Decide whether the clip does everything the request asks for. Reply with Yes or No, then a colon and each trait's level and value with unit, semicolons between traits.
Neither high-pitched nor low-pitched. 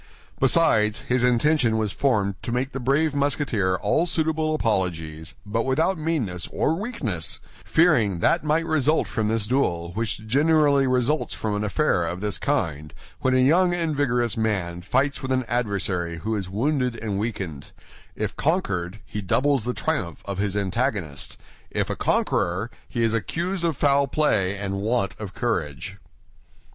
No: low, 115 Hz